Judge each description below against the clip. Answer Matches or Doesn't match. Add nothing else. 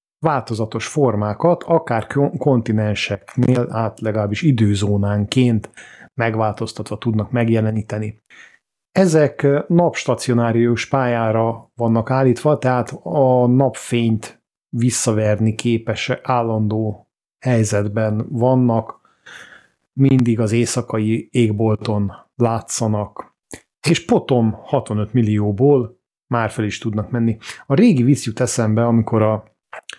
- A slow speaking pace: Matches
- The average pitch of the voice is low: Matches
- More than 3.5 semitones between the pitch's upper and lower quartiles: Doesn't match